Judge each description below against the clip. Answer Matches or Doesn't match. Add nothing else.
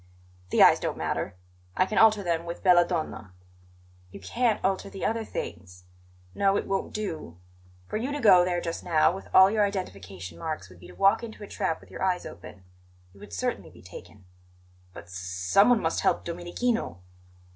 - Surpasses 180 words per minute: Matches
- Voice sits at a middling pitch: Matches